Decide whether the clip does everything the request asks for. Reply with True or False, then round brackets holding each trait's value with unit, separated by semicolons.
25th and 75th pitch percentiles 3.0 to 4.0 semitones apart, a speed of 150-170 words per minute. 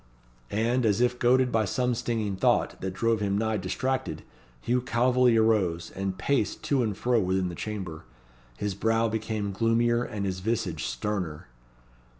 True (3.7 semitones; 155 wpm)